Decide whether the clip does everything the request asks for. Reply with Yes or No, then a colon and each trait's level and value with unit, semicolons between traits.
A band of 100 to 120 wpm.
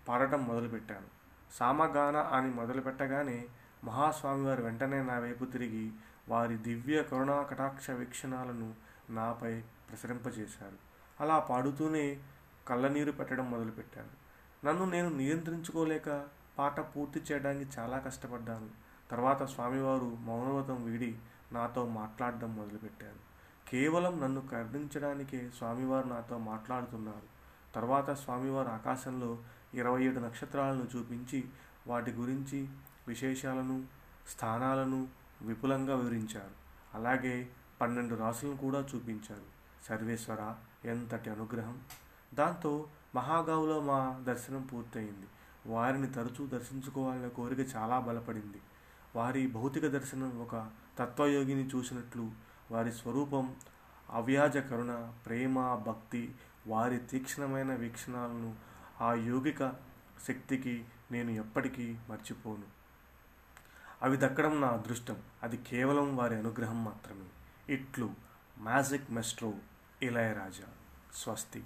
No: average, 90 wpm